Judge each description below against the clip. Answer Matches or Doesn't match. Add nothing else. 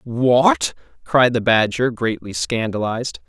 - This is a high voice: Doesn't match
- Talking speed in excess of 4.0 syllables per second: Doesn't match